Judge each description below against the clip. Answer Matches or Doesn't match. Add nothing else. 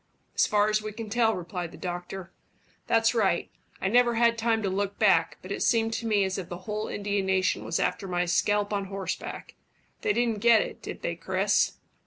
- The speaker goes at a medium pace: Doesn't match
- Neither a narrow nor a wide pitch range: Matches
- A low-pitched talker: Doesn't match